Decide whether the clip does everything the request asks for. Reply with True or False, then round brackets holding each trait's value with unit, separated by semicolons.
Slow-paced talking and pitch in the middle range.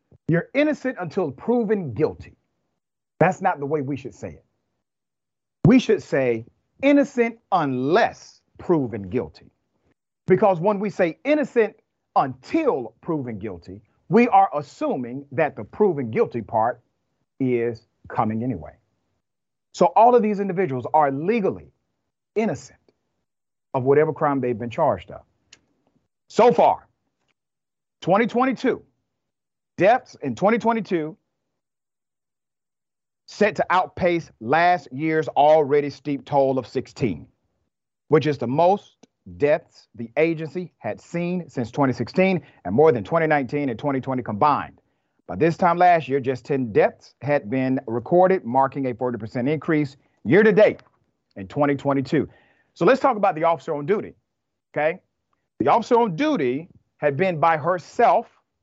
True (130 wpm; 155 Hz)